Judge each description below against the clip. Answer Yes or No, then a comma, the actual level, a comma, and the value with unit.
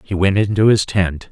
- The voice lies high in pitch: No, very low, 95 Hz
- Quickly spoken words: Yes, fast, 230 wpm